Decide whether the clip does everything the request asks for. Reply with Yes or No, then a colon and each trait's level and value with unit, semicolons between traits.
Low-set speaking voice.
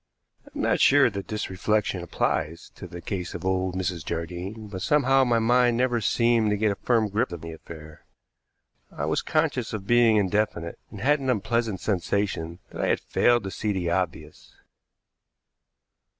Yes: low, 105 Hz